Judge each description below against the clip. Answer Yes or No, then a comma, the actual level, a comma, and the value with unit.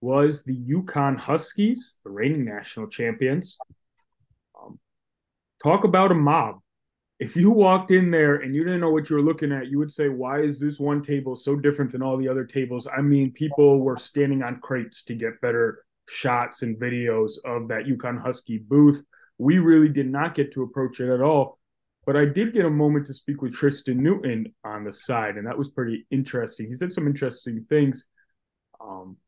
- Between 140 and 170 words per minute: No, average, 195 wpm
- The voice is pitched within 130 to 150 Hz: Yes, medium, 140 Hz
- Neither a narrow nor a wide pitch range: Yes, average, 3.1 semitones